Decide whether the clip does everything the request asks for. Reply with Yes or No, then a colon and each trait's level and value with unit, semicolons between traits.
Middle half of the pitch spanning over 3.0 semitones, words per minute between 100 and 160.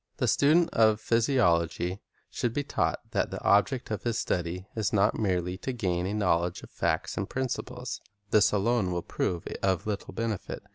No: average, 4.7 semitones; average, 180 wpm